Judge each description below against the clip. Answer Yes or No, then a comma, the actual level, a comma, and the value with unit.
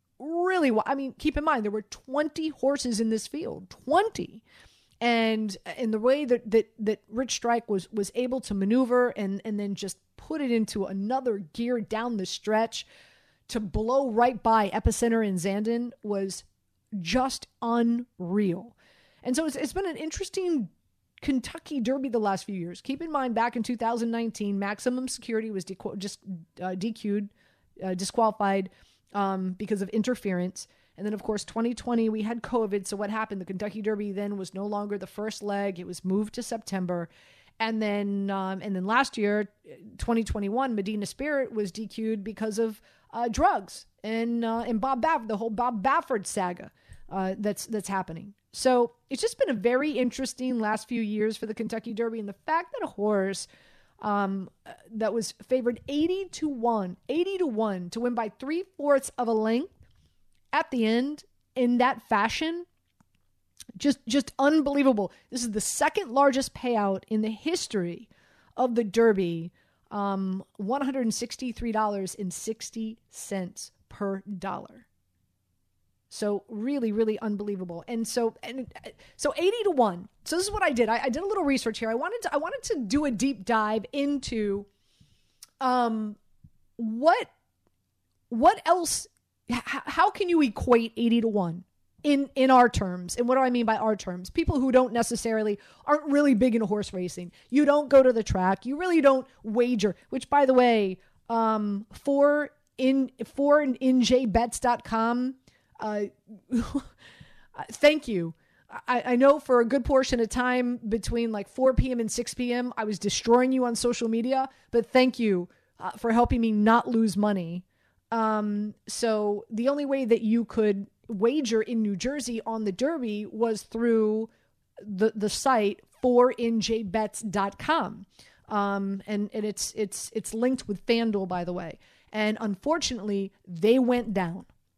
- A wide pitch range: No, average, 3.8 semitones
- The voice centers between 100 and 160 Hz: No, high, 225 Hz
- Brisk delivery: No, average, 160 wpm